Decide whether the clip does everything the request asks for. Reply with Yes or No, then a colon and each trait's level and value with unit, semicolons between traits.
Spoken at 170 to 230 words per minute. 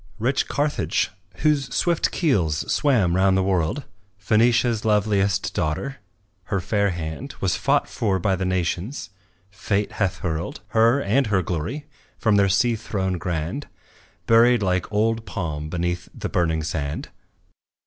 No: average, 140 wpm